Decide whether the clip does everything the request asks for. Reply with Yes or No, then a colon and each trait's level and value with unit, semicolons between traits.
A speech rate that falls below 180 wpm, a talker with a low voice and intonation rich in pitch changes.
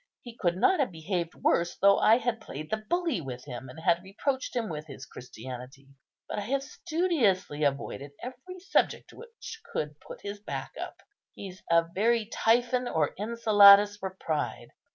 No: average, 170 wpm; high, 200 Hz; wide, 7.7 semitones